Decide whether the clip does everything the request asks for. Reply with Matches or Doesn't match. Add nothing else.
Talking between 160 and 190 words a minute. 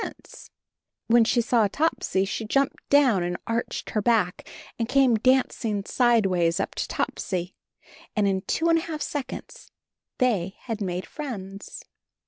Doesn't match